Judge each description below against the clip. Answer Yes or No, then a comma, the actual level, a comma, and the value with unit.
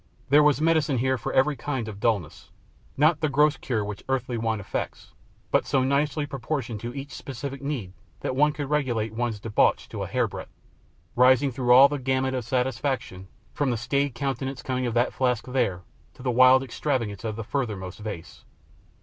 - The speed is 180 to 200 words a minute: Yes, average, 185 wpm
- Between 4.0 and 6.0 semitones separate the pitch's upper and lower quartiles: No, average, 3.4 semitones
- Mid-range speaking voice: No, low, 130 Hz